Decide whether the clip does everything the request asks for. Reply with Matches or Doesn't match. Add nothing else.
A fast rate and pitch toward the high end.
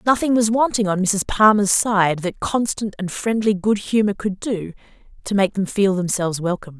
Doesn't match